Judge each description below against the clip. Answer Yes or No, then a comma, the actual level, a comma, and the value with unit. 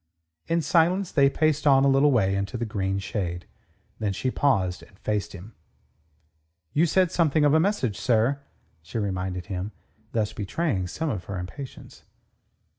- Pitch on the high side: No, low, 115 Hz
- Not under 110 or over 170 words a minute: Yes, average, 160 wpm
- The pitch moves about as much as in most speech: No, wide, 7.2 semitones